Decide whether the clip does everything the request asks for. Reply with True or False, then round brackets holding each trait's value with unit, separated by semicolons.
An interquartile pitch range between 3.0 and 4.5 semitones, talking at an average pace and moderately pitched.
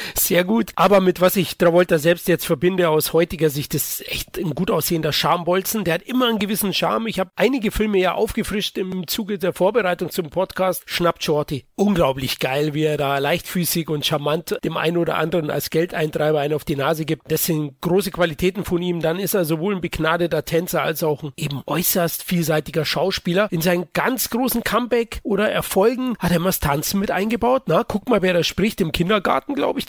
False (3.3 semitones; 205 wpm; 175 Hz)